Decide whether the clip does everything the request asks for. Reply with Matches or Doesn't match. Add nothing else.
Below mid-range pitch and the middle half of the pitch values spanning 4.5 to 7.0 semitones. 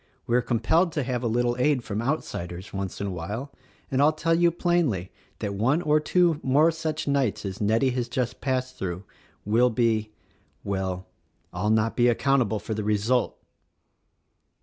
Matches